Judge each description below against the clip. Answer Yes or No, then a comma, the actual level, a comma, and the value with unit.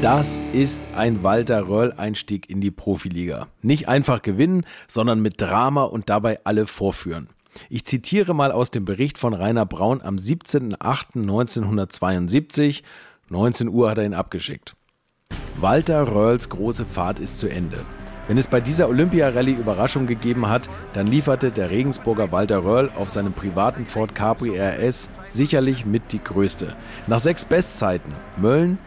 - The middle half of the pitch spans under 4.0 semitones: No, average, 4.6 semitones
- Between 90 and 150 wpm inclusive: Yes, average, 145 wpm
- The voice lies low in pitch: Yes, low, 115 Hz